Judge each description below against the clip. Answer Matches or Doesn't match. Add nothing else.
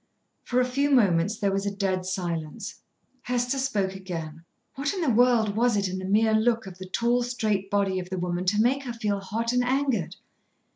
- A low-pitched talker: Doesn't match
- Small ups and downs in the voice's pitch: Doesn't match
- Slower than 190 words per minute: Doesn't match